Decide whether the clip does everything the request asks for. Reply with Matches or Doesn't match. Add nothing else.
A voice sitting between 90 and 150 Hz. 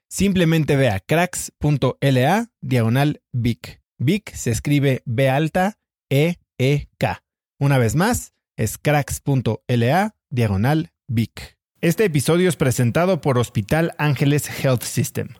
Matches